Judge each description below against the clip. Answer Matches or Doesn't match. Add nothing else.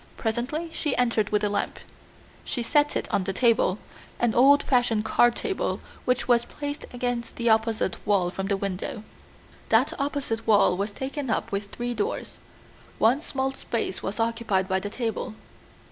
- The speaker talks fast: Doesn't match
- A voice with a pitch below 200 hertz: Doesn't match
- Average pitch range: Matches